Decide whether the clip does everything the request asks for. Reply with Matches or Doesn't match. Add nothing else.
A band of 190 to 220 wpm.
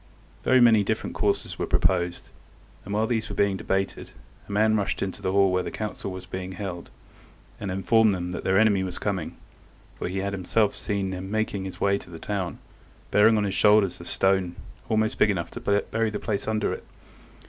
Matches